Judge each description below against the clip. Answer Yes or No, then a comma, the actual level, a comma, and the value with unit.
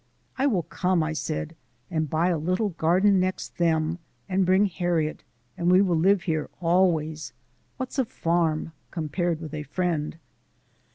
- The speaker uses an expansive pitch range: No, average, 2.8 semitones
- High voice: No, medium, 170 Hz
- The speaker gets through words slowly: No, average, 155 wpm